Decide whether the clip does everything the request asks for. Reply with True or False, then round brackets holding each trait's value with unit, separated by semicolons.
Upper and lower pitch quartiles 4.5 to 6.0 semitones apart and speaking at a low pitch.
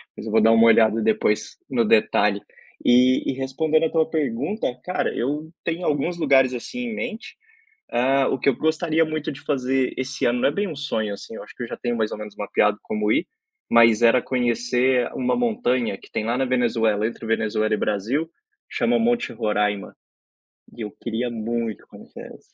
True (4.9 semitones; 125 Hz)